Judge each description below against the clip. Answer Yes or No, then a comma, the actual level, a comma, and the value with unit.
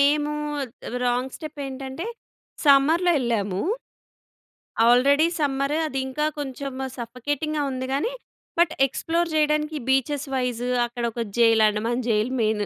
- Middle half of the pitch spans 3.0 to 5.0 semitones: Yes, average, 3.6 semitones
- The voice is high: Yes, very high, 270 Hz